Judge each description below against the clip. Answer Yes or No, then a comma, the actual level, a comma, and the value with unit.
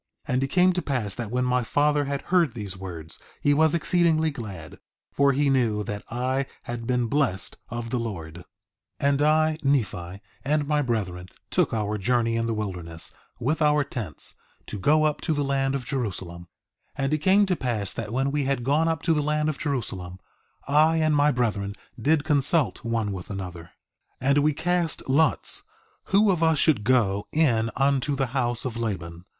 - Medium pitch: No, low, 130 Hz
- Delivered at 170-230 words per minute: Yes, average, 190 wpm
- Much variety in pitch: Yes, wide, 5.8 semitones